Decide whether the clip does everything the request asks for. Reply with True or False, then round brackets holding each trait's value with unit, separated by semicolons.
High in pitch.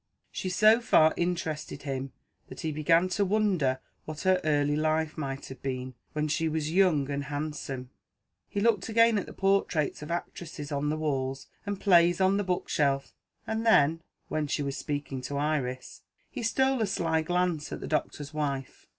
False (155 Hz)